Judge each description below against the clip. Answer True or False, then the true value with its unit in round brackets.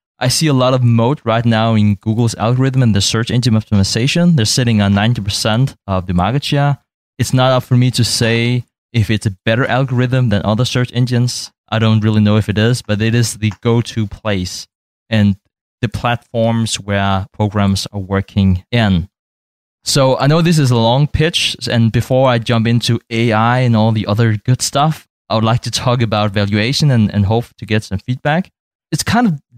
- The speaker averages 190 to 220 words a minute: True (200 wpm)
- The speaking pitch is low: True (115 Hz)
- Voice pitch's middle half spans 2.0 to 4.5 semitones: True (3.1 semitones)